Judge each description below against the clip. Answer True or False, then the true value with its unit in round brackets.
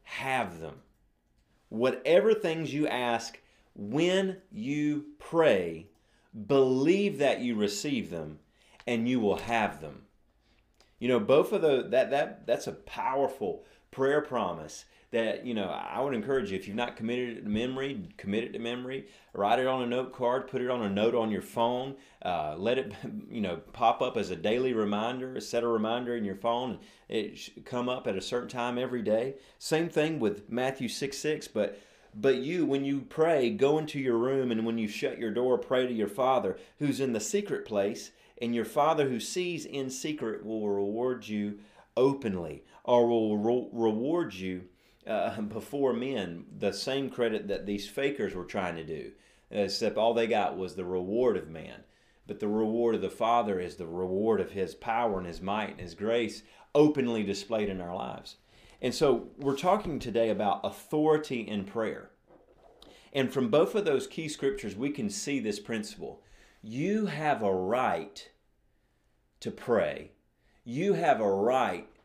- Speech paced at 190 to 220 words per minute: False (180 wpm)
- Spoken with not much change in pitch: False (4.3 semitones)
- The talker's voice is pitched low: True (125 Hz)